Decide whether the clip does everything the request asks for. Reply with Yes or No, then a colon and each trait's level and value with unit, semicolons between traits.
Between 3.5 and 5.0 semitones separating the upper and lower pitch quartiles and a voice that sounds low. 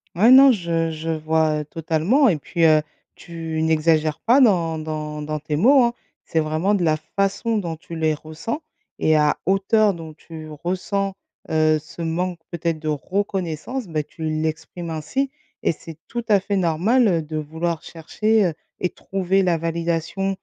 No: average, 3.8 semitones; medium, 165 Hz